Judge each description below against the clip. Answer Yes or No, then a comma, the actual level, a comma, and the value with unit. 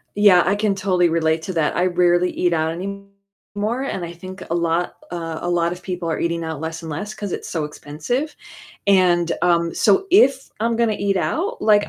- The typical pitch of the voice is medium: Yes, medium, 180 Hz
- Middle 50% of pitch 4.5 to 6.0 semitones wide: No, average, 3.2 semitones